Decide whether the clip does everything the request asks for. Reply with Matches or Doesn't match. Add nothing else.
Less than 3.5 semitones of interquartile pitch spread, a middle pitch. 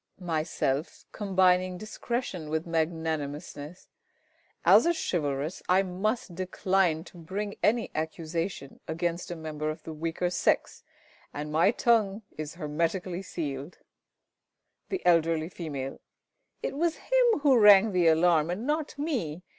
Doesn't match